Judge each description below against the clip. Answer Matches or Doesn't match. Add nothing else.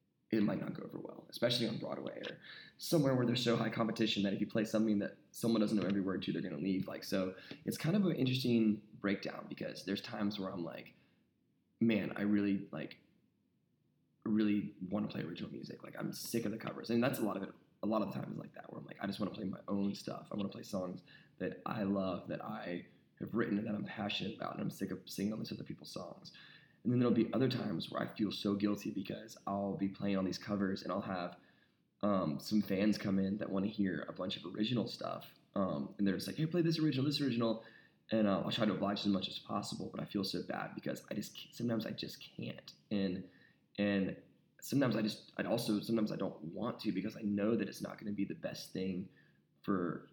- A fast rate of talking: Matches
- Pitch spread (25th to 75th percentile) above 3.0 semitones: Doesn't match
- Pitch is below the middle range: Matches